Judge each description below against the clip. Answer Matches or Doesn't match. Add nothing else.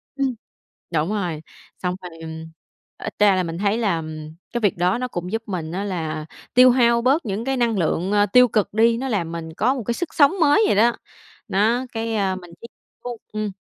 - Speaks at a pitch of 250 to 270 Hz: Doesn't match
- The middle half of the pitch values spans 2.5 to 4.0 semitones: Doesn't match